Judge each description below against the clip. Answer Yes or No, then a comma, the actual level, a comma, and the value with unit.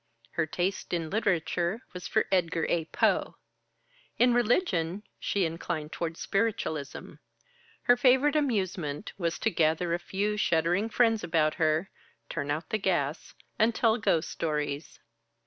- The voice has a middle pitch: Yes, medium, 175 Hz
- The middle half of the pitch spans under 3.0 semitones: No, average, 5.1 semitones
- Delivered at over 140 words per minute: No, slow, 135 wpm